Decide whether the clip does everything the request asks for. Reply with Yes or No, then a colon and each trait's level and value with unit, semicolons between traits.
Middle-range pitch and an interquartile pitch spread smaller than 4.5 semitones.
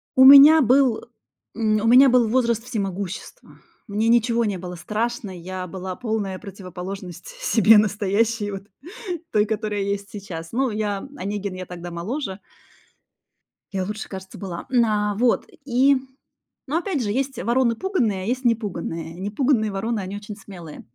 No: high, 210 Hz; average, 3.8 semitones